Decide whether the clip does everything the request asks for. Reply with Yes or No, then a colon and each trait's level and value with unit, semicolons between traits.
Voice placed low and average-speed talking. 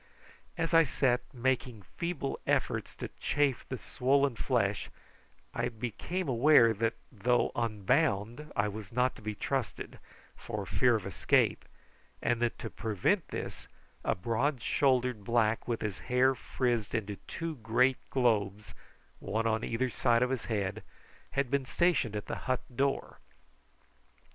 Yes: low, 120 Hz; average, 145 wpm